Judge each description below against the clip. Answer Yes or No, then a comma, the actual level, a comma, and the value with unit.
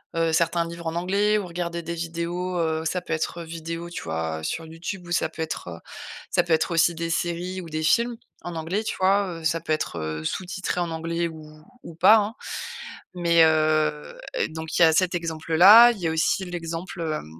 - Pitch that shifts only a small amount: Yes, narrow, 1.8 semitones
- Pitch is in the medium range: Yes, medium, 170 Hz